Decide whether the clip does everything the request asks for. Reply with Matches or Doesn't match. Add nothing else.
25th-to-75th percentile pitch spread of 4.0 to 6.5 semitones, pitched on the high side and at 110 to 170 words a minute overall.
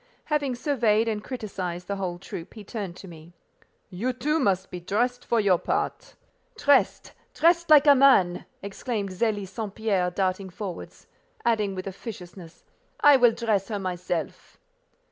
Matches